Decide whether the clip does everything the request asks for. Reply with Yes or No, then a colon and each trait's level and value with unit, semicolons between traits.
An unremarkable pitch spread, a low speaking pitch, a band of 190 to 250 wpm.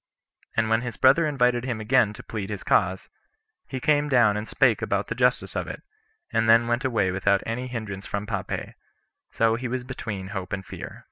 Yes: average, 3.5 semitones; low, 115 Hz; average, 200 wpm